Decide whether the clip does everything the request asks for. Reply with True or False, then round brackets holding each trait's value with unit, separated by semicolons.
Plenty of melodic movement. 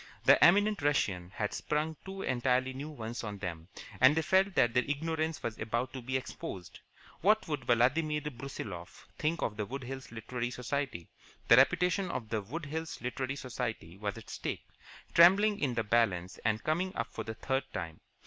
True (5.7 semitones)